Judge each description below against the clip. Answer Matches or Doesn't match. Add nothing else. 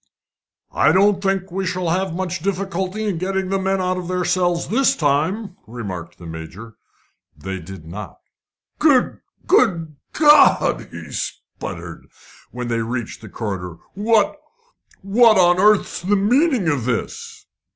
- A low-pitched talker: Doesn't match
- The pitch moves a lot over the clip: Matches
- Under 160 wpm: Matches